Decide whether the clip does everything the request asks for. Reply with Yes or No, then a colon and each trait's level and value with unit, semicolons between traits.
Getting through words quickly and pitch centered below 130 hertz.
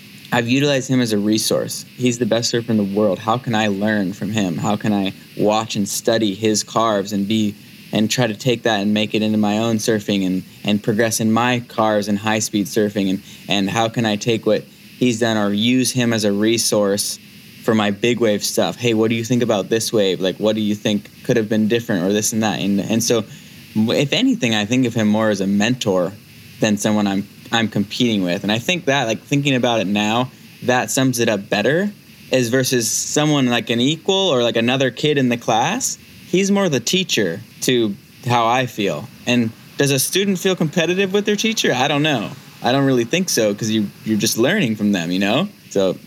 Yes: fast, 225 wpm; low, 115 Hz